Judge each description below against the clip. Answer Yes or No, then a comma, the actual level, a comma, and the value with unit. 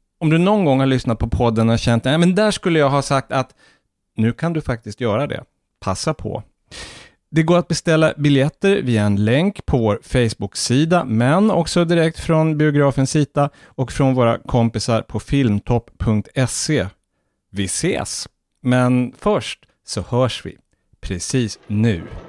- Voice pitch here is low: Yes, low, 130 Hz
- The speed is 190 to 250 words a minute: No, average, 155 wpm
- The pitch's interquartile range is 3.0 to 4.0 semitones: No, wide, 5.4 semitones